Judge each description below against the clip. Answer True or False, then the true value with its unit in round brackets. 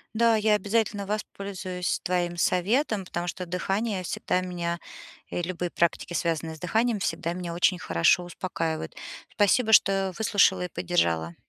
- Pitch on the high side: False (180 Hz)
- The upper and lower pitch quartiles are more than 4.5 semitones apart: False (2.8 semitones)